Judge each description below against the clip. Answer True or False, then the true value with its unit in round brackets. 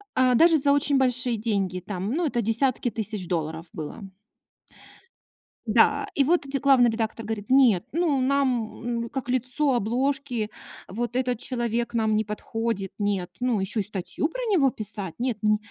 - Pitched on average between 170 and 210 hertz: False (235 Hz)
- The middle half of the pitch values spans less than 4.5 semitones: True (4.1 semitones)